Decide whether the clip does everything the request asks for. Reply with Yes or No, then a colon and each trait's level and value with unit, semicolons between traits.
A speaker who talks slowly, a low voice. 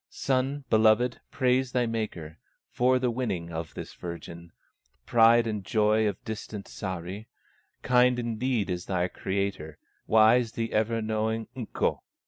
Yes: slow, 130 wpm; low, 110 Hz